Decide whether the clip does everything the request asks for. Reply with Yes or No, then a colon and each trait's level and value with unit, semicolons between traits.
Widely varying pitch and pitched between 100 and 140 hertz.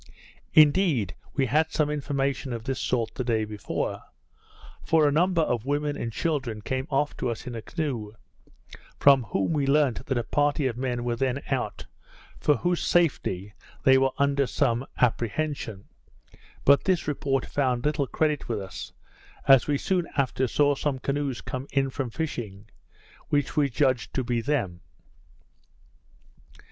No: average, 3.5 semitones; low, 135 Hz